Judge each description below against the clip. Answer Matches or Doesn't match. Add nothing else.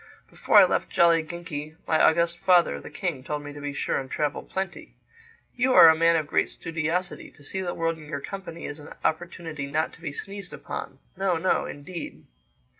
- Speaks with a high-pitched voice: Doesn't match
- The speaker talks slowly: Doesn't match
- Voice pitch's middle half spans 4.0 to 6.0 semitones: Doesn't match